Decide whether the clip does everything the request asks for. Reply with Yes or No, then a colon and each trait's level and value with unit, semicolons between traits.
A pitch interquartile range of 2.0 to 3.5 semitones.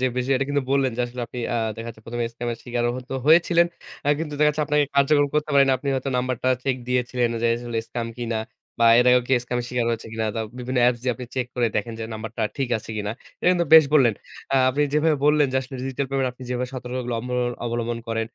Yes: average, 2.8 semitones